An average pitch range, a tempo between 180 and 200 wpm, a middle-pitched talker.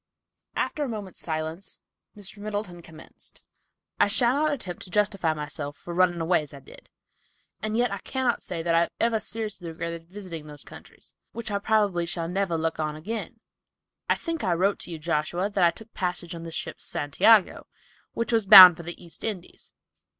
Yes: average, 4.3 semitones; average, 190 wpm; medium, 180 Hz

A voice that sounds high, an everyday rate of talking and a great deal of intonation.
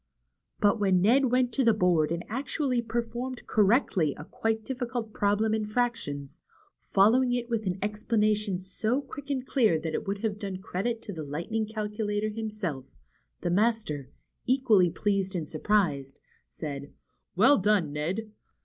No: high, 210 Hz; average, 160 wpm; average, 4.3 semitones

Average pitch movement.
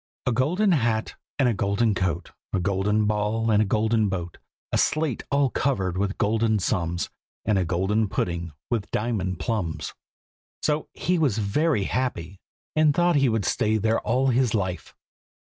Yes: average, 4.7 semitones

